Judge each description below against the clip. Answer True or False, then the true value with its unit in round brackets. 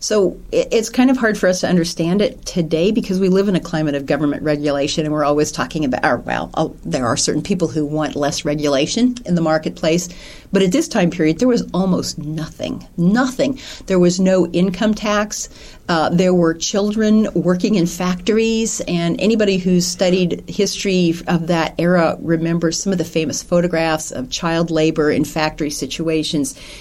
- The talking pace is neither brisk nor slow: True (175 wpm)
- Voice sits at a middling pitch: True (175 Hz)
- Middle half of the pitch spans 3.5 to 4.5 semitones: True (3.9 semitones)